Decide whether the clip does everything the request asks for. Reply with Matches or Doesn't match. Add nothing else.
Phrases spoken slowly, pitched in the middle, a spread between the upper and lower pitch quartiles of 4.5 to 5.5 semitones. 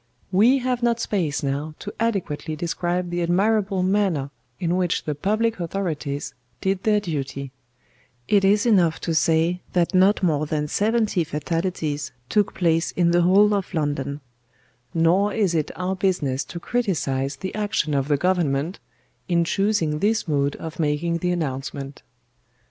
Doesn't match